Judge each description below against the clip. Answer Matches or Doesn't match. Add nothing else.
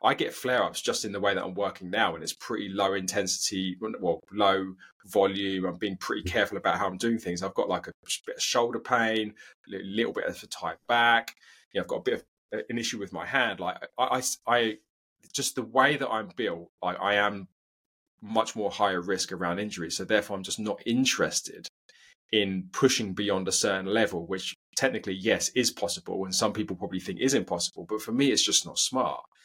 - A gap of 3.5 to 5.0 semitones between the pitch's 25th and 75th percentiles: Doesn't match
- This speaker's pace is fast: Matches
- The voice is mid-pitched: Doesn't match